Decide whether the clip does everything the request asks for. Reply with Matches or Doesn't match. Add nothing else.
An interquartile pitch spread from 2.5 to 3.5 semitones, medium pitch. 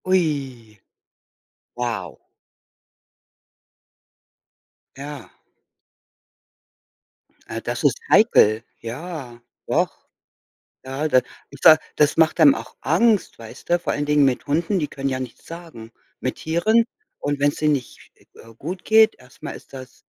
Doesn't match